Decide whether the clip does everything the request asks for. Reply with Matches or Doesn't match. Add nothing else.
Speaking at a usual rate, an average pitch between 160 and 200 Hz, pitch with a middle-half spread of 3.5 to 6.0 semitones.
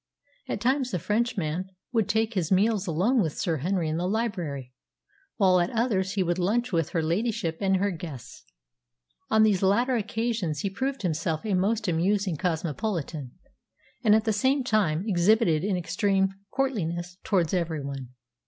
Matches